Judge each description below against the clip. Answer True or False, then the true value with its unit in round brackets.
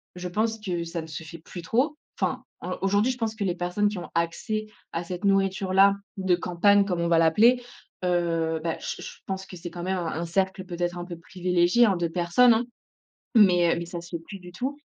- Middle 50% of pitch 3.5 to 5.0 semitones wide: False (2.8 semitones)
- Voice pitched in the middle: True (180 Hz)